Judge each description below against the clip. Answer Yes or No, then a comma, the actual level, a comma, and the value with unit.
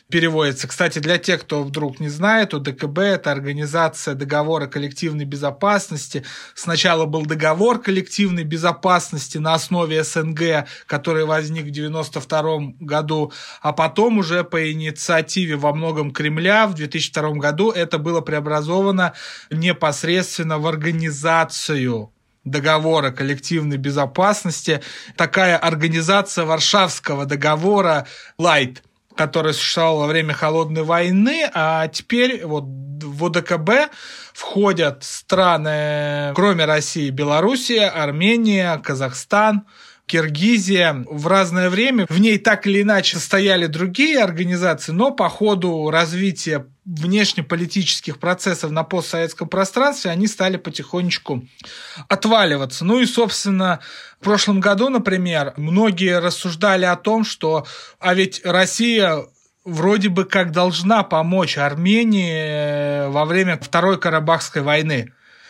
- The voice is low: No, medium, 165 Hz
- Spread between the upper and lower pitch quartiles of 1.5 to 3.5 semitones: No, average, 3.9 semitones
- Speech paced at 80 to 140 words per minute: Yes, slow, 110 wpm